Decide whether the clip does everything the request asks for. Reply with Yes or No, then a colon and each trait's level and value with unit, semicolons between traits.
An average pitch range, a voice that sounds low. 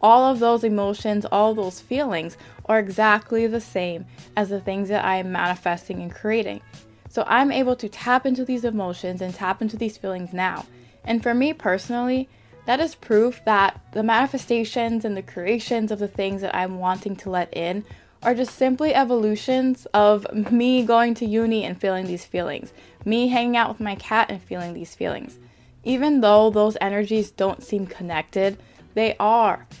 No: average, 3.8 semitones; high, 215 Hz